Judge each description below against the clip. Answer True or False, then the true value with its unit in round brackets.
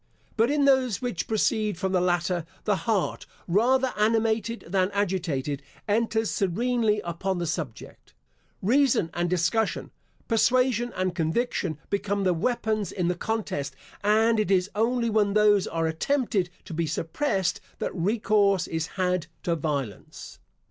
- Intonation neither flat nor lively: True (4.5 semitones)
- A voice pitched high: True (200 Hz)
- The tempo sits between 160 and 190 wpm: False (140 wpm)